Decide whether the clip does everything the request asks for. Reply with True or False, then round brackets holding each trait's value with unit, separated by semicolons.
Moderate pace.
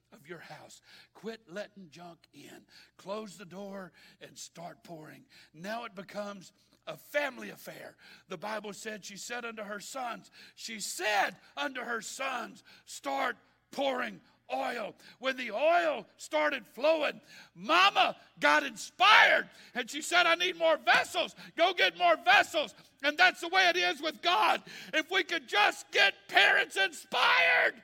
True (150 wpm)